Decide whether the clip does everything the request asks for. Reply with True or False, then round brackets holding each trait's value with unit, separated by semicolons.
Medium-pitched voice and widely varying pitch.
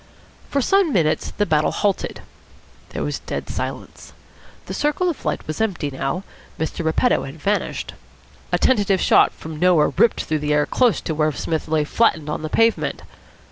True (165 Hz; 6.4 semitones)